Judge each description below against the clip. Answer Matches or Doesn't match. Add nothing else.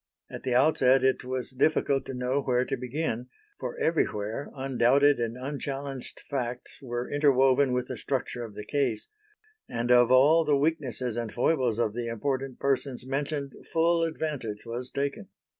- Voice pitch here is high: Doesn't match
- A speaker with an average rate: Matches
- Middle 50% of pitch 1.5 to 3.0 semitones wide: Matches